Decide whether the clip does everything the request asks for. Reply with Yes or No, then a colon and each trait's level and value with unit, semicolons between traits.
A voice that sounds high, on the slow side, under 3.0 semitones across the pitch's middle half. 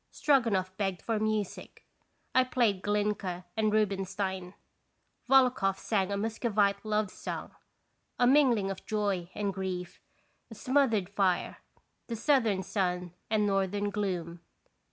Yes: high, 205 Hz; slow, 120 wpm; narrow, 2.5 semitones